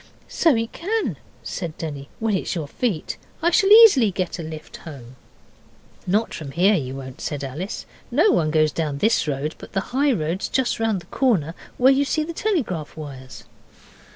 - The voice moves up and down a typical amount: No, wide, 8.7 semitones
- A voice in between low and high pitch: Yes, medium, 180 Hz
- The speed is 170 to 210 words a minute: Yes, average, 180 wpm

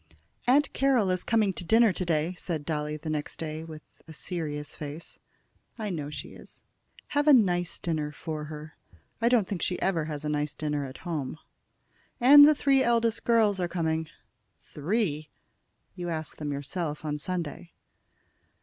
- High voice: No, medium, 165 Hz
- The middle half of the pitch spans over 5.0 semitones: Yes, wide, 5.4 semitones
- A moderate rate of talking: Yes, average, 165 wpm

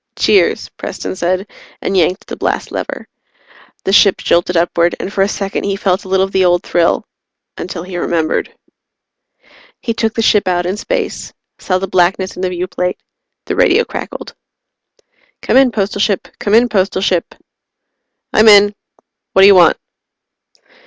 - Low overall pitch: No, high, 190 Hz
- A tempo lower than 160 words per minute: No, average, 165 wpm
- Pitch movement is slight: Yes, narrow, 2.3 semitones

